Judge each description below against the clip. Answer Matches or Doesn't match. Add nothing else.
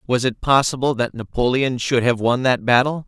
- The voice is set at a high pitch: Doesn't match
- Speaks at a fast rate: Doesn't match